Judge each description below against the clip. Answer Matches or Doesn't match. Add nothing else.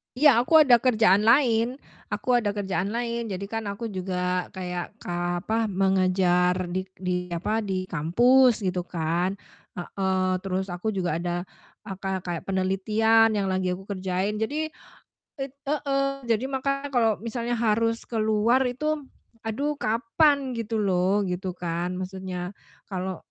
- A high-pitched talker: Matches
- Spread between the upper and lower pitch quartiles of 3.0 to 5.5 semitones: Matches